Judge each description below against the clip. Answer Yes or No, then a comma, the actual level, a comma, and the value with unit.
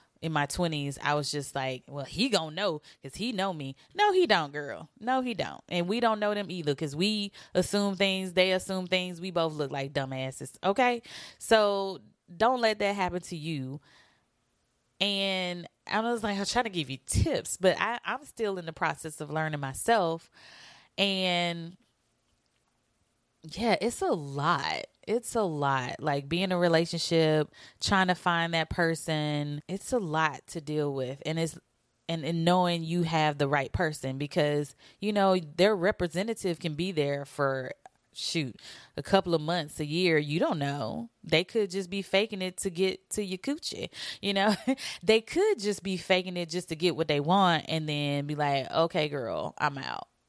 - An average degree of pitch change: Yes, average, 4.8 semitones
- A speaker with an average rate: Yes, average, 185 wpm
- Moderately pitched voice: Yes, medium, 170 Hz